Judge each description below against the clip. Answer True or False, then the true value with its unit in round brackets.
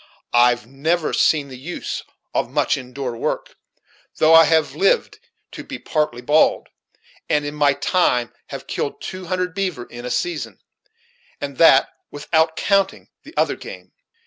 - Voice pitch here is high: False (150 Hz)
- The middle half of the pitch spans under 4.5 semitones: False (4.8 semitones)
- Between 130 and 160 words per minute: True (155 wpm)